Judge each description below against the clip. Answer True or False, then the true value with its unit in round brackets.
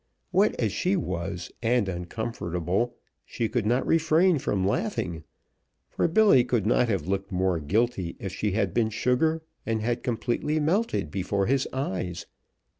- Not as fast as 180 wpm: True (150 wpm)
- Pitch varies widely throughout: True (6.3 semitones)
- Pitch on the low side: True (115 Hz)